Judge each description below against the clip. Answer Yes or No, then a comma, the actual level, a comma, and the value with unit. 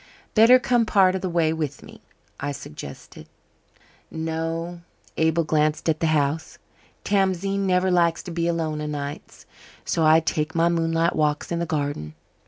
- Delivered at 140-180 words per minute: Yes, average, 160 wpm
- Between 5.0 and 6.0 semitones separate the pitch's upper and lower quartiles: No, narrow, 2.4 semitones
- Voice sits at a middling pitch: Yes, medium, 165 Hz